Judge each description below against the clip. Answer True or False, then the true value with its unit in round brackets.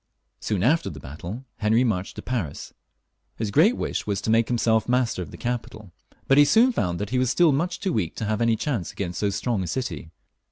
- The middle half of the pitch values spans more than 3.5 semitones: True (4.7 semitones)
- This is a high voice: False (110 Hz)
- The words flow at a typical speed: False (225 wpm)